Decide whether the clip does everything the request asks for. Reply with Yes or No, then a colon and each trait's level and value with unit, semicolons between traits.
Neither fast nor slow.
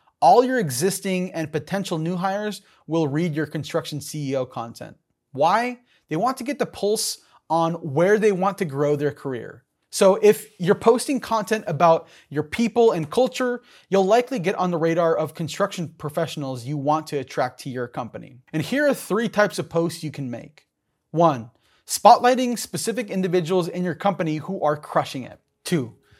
Yes: average, 175 wpm